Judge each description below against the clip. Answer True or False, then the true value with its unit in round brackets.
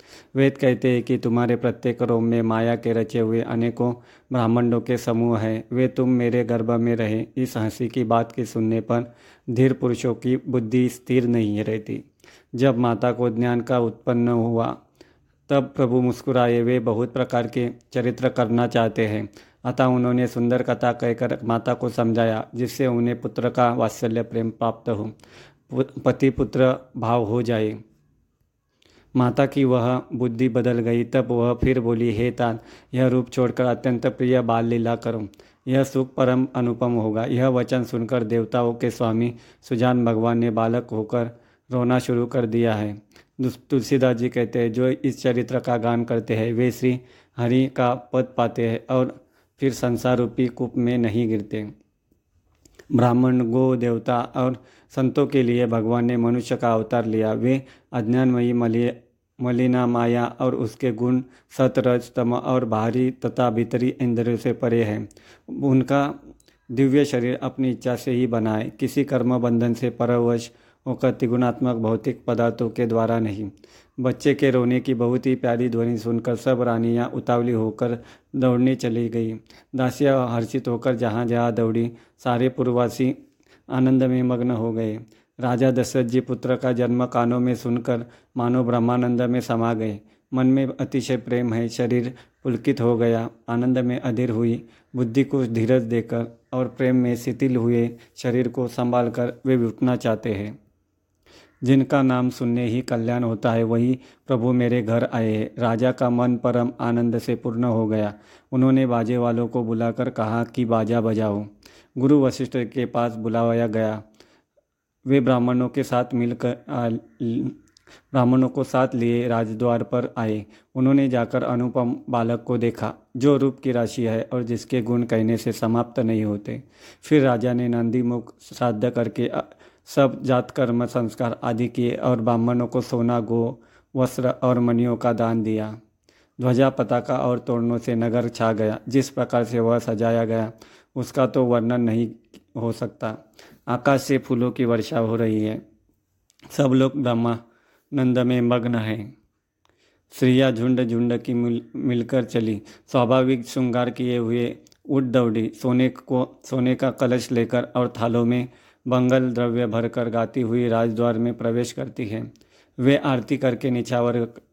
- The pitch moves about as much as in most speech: False (1.5 semitones)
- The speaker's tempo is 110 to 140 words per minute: False (155 wpm)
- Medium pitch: False (120 Hz)